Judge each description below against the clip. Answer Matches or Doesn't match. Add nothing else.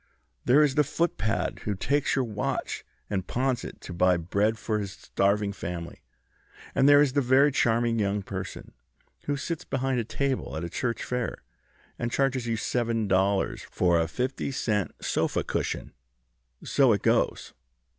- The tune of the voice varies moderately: Matches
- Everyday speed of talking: Matches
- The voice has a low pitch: Matches